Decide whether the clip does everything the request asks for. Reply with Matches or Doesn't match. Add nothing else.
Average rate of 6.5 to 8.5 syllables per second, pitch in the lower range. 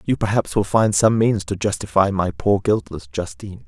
Doesn't match